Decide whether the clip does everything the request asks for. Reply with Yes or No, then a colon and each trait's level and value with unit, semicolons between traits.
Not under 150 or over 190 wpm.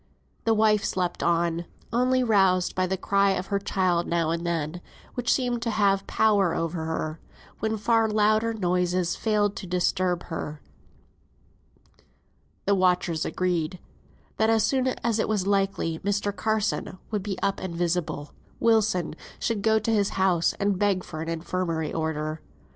Yes: average, 155 wpm